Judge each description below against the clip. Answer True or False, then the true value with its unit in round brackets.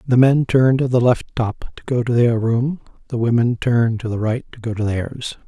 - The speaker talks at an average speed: False (240 wpm)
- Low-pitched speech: True (120 Hz)